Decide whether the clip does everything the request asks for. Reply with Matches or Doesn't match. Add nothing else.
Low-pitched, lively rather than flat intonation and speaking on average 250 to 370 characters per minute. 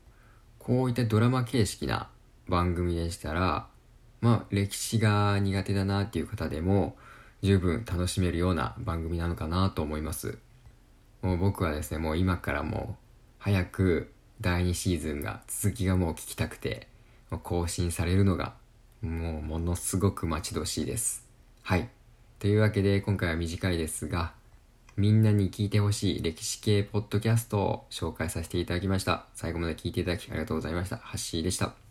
Doesn't match